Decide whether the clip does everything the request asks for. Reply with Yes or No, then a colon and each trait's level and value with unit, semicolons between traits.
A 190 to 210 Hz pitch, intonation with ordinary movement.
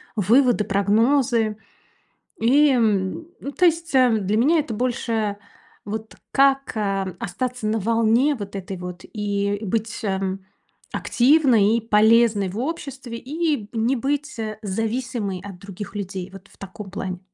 No: high, 220 Hz; average, 4.2 semitones